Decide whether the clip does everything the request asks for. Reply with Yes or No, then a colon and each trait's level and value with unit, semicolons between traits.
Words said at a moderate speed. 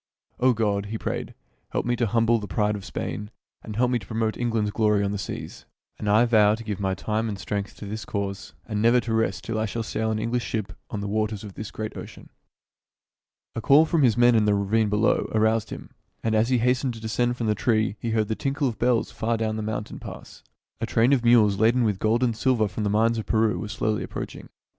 No: fast, 240 wpm